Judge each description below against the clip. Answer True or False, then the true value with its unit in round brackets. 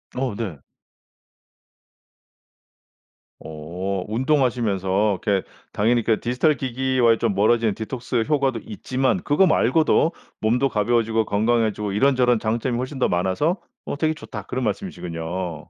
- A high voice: False (115 Hz)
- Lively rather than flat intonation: False (4.2 semitones)